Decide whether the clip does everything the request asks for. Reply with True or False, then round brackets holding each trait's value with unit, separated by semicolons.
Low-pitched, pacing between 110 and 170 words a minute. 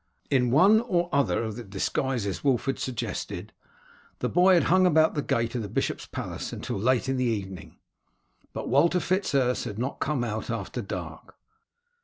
False (130 Hz; 180 wpm)